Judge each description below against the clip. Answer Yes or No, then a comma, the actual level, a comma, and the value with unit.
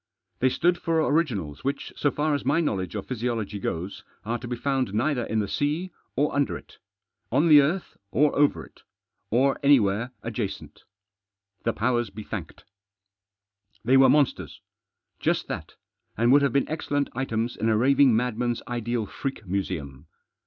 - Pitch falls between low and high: No, low, 125 Hz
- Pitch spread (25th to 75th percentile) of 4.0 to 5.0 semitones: Yes, average, 4.7 semitones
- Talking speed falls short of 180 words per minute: Yes, average, 160 wpm